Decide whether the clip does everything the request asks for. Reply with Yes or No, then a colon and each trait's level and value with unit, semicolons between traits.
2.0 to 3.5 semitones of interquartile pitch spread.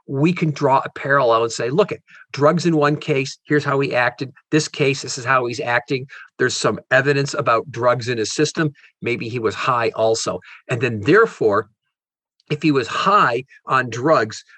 Yes: average, 2.7 semitones